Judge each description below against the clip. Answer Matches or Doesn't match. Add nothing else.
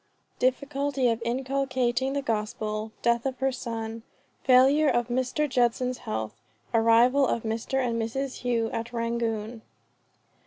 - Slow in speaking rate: Matches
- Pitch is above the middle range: Matches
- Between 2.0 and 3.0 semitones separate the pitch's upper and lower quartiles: Matches